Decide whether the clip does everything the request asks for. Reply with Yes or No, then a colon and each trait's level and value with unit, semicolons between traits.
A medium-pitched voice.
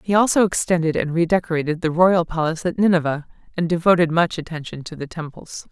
Yes: medium, 170 Hz